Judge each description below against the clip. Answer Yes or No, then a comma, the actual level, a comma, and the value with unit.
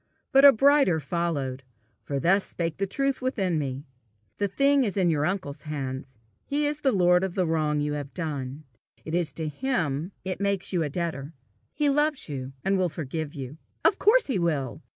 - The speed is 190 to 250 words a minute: Yes, average, 195 wpm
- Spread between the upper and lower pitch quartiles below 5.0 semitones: No, wide, 5.5 semitones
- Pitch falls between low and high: Yes, medium, 170 Hz